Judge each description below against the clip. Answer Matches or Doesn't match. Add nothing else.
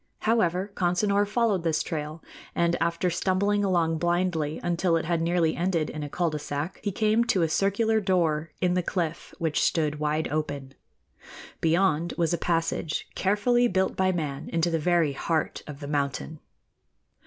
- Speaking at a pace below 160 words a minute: Doesn't match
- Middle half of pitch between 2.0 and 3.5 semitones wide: Matches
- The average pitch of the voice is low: Doesn't match